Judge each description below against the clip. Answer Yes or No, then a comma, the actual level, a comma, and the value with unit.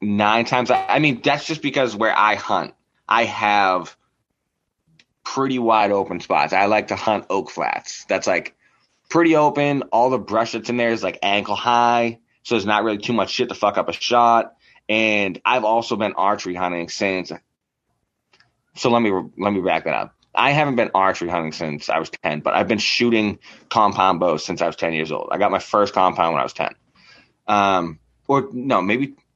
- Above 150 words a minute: Yes, average, 200 wpm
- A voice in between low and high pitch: No, low, 110 Hz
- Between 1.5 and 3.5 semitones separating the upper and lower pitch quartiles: No, average, 4.5 semitones